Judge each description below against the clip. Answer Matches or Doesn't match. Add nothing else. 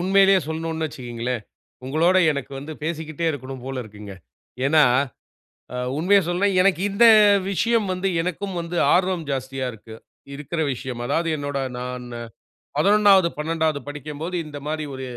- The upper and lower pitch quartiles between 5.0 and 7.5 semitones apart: Matches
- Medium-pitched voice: Matches